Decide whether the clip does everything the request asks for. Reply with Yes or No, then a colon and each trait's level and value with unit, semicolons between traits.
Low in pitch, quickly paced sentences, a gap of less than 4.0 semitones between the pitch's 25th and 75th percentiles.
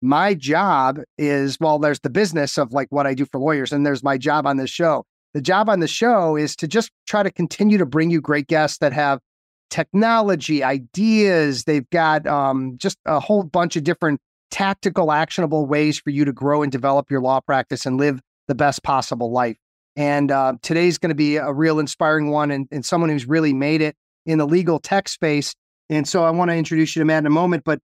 No: medium, 150 Hz; fast, 220 wpm; average, 2.9 semitones